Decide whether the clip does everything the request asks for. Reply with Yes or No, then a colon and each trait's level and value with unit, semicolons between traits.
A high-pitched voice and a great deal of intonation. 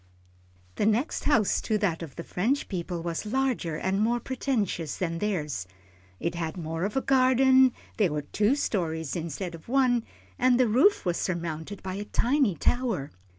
Yes: high, 200 Hz; wide, 7.0 semitones